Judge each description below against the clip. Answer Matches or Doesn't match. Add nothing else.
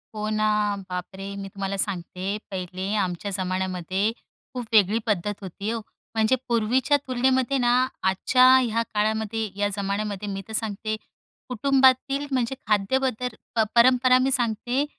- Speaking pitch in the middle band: Doesn't match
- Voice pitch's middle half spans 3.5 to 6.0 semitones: Matches